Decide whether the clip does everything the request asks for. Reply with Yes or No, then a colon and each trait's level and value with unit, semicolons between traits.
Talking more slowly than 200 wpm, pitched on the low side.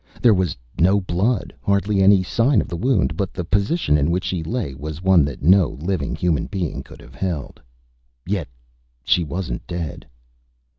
Yes: average, 170 wpm; very low, 90 Hz